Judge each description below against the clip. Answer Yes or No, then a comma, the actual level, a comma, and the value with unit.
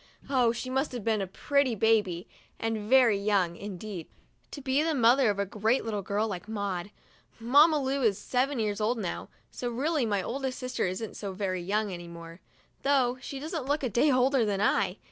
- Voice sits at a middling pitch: No, high, 225 Hz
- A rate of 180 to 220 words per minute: Yes, average, 195 wpm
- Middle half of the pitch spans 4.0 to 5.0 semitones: Yes, average, 4.7 semitones